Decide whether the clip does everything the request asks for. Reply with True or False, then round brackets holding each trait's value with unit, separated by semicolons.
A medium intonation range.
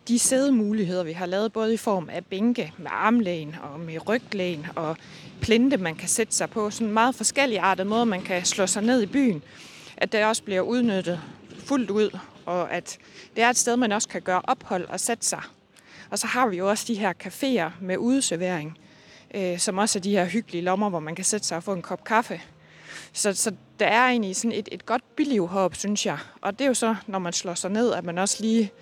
True (4.0 semitones)